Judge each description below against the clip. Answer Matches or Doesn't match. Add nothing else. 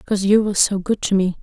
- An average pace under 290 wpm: Doesn't match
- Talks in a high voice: Matches